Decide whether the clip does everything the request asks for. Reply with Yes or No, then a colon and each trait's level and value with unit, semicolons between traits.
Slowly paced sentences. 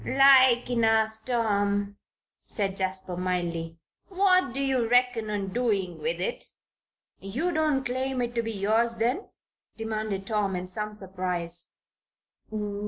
Yes: slow, 125 wpm